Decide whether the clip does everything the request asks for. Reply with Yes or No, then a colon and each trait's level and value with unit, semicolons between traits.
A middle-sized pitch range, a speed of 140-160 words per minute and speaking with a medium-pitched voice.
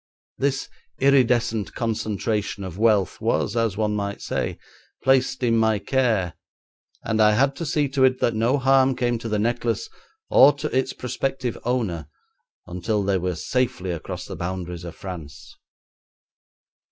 No: average, 4.5 semitones; average, 150 wpm; low, 115 Hz